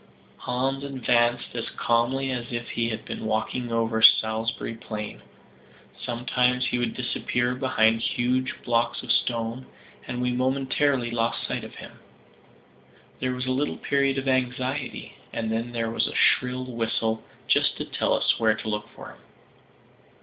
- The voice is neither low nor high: No, low, 120 Hz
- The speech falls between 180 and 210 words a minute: No, average, 155 wpm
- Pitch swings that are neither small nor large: No, narrow, 1.9 semitones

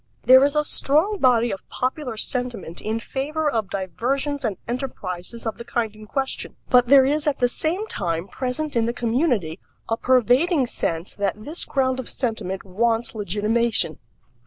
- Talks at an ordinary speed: Yes, average, 165 wpm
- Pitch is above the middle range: Yes, high, 240 Hz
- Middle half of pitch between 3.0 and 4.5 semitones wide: Yes, average, 4.2 semitones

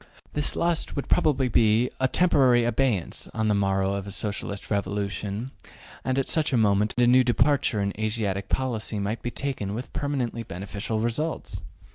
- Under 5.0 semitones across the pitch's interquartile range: Yes, average, 4.3 semitones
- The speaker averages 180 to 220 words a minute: No, average, 165 wpm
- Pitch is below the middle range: Yes, low, 115 Hz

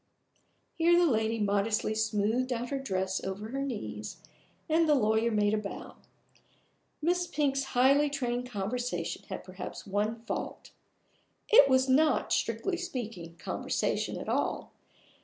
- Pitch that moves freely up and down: No, average, 5.0 semitones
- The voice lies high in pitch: Yes, high, 235 Hz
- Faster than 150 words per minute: No, slow, 135 wpm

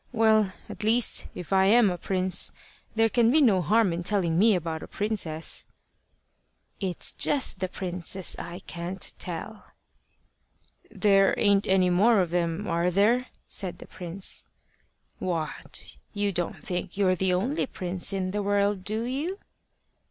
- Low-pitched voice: No, high, 195 Hz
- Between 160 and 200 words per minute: No, average, 150 wpm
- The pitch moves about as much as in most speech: Yes, average, 3.2 semitones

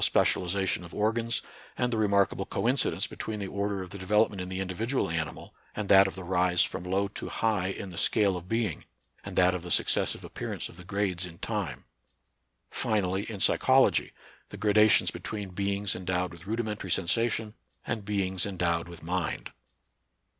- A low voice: Yes, very low, 95 Hz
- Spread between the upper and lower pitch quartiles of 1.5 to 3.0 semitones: Yes, average, 2.7 semitones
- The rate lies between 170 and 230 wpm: Yes, average, 180 wpm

